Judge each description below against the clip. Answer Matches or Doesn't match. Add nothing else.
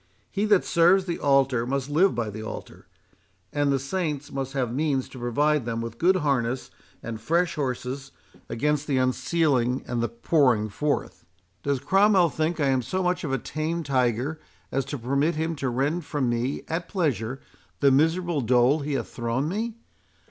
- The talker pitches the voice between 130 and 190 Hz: Matches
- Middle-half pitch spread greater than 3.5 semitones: Matches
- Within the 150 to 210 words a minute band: Matches